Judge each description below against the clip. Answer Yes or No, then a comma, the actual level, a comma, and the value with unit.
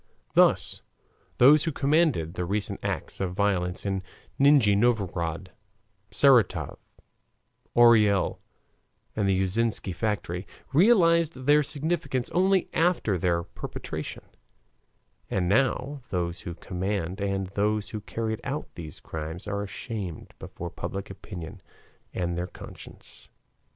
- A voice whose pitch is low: Yes, low, 100 Hz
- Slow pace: Yes, slow, 115 wpm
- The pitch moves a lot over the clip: Yes, wide, 6.7 semitones